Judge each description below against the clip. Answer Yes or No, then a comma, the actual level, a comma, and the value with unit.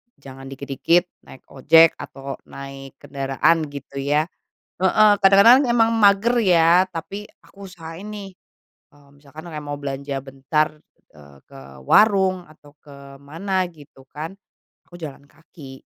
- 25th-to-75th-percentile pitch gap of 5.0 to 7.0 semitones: Yes, wide, 5.4 semitones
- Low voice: No, medium, 155 Hz